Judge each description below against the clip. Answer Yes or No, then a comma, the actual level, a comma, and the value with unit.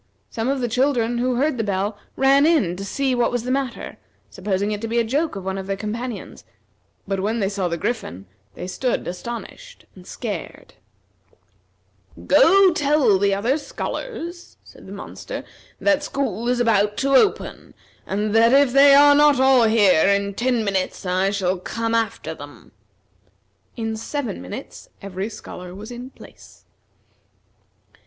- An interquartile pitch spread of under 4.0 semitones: No, average, 5.1 semitones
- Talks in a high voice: Yes, high, 230 Hz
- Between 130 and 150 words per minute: No, average, 160 wpm